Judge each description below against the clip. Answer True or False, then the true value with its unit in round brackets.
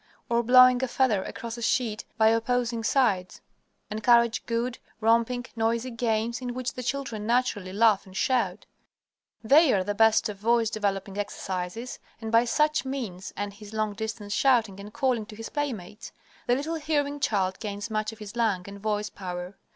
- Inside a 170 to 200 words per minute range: True (175 wpm)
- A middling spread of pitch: True (3.2 semitones)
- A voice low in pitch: False (225 Hz)